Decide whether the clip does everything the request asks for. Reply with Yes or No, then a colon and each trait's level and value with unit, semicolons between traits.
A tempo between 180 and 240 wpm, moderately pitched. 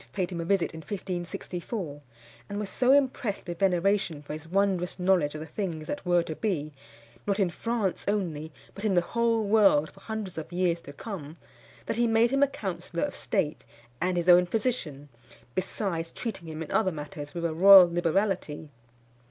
Yes: average, 185 wpm; medium, 180 Hz